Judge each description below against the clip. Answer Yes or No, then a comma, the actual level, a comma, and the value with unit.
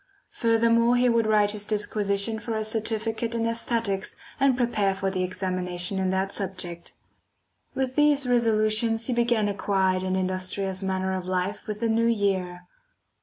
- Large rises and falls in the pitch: No, average, 3.4 semitones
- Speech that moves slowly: No, average, 160 wpm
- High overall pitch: Yes, high, 210 Hz